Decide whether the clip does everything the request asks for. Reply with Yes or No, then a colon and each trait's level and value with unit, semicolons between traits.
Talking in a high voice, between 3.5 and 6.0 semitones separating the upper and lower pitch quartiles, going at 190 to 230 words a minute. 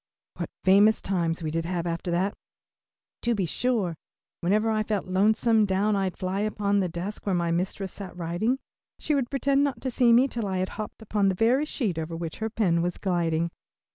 Yes: high, 195 Hz; average, 4.0 semitones; average, 200 wpm